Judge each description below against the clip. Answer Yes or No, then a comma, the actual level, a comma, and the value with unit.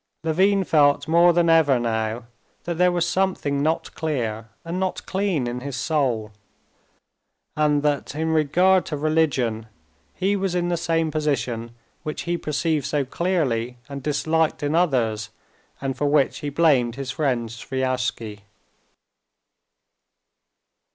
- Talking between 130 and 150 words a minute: Yes, slow, 135 wpm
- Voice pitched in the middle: Yes, medium, 150 Hz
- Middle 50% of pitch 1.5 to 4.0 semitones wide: No, average, 4.8 semitones